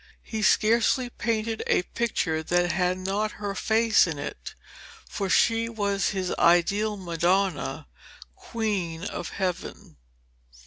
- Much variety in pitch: No, average, 3.8 semitones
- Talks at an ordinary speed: No, slow, 120 wpm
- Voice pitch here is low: No, high, 200 Hz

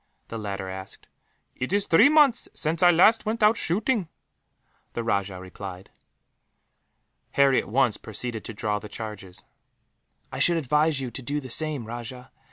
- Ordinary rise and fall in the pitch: No, wide, 7.9 semitones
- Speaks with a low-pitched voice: Yes, low, 130 Hz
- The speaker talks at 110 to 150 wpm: No, average, 160 wpm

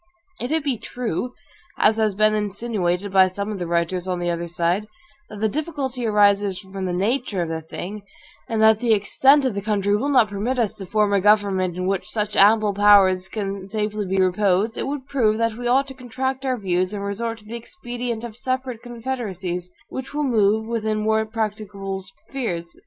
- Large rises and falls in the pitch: No, average, 3.6 semitones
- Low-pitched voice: No, high, 210 Hz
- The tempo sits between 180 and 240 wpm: Yes, average, 200 wpm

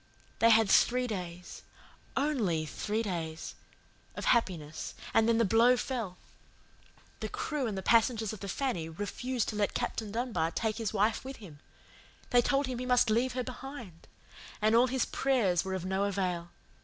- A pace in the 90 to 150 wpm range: No, average, 170 wpm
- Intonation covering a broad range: No, average, 4.8 semitones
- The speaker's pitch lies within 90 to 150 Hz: No, high, 220 Hz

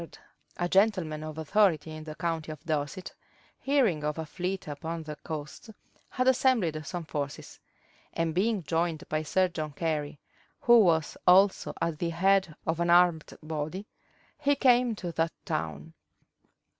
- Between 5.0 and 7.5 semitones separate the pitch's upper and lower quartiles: No, average, 3.6 semitones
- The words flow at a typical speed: Yes, average, 160 wpm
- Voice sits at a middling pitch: Yes, medium, 165 Hz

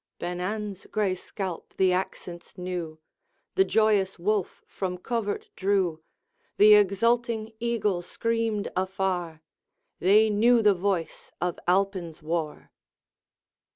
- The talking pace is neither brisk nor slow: No, slow, 110 wpm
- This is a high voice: Yes, high, 195 Hz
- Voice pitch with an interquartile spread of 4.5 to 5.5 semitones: No, average, 3.1 semitones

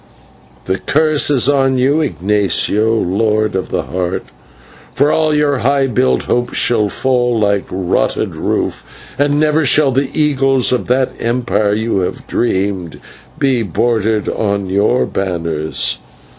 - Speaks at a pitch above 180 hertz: No, low, 115 Hz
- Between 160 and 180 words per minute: No, average, 145 wpm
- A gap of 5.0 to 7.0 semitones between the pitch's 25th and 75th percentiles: Yes, average, 5.3 semitones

